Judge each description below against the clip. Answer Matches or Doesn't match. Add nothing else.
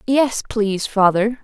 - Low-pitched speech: Doesn't match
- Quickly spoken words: Doesn't match